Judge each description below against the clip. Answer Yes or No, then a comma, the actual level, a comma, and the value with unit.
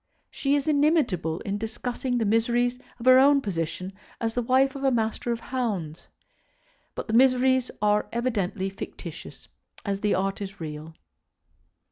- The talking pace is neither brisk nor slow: Yes, average, 155 wpm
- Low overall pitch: No, high, 230 Hz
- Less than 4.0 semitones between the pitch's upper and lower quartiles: No, average, 4.6 semitones